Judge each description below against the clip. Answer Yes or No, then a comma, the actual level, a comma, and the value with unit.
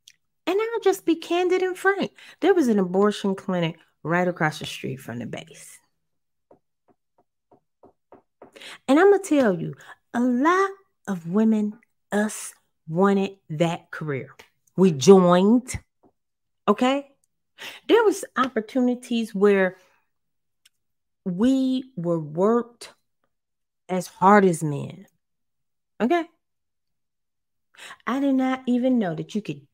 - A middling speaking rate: No, slow, 115 wpm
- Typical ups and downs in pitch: No, wide, 6.7 semitones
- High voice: Yes, high, 210 Hz